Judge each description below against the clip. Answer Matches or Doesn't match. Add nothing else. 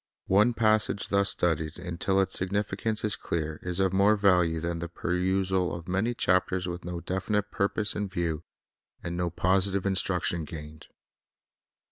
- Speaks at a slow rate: Doesn't match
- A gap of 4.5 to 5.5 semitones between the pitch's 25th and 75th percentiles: Doesn't match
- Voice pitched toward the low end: Matches